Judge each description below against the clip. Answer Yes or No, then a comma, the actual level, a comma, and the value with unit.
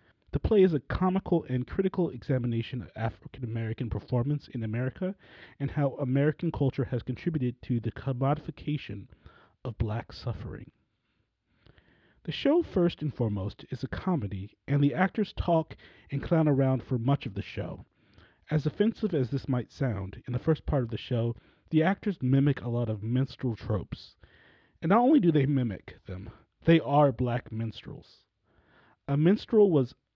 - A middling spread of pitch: Yes, average, 5.0 semitones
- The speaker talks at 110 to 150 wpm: No, average, 160 wpm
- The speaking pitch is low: Yes, low, 130 Hz